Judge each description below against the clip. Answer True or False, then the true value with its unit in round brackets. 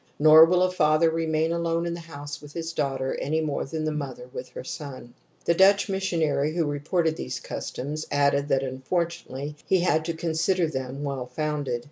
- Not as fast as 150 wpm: False (185 wpm)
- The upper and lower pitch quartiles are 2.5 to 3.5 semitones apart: True (2.9 semitones)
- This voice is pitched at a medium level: True (155 Hz)